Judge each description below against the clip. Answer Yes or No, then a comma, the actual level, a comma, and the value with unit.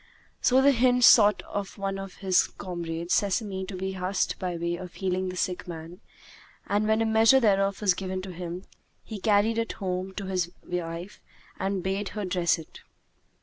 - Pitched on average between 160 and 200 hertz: Yes, high, 190 Hz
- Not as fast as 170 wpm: No, average, 185 wpm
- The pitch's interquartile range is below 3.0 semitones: Yes, narrow, 2.4 semitones